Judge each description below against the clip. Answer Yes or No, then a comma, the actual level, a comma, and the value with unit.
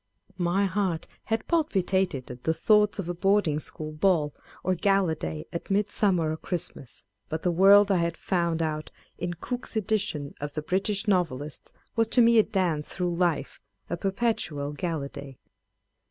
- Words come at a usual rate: Yes, average, 170 wpm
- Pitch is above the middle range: No, medium, 175 Hz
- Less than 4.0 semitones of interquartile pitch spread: No, average, 4.4 semitones